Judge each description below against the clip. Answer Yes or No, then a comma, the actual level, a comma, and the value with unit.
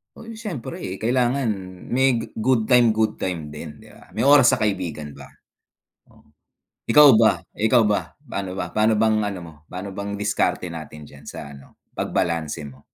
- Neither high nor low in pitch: No, low, 105 Hz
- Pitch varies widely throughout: Yes, wide, 6.8 semitones